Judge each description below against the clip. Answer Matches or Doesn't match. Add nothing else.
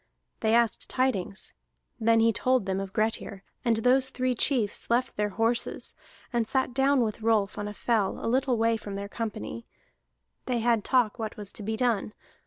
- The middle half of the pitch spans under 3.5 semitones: Matches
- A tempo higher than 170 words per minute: Matches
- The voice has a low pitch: Doesn't match